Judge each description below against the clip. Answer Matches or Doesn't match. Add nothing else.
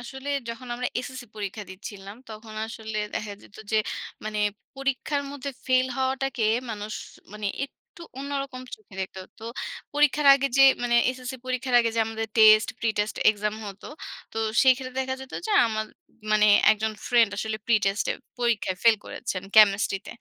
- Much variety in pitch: Doesn't match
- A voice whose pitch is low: Doesn't match